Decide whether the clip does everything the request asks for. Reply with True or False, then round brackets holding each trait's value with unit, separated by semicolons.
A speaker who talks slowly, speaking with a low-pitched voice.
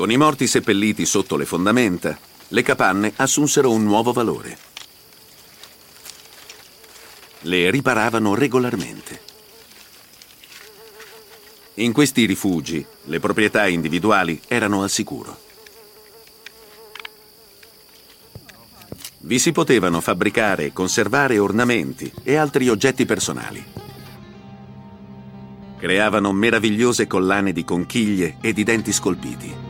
True (90 wpm; 105 Hz)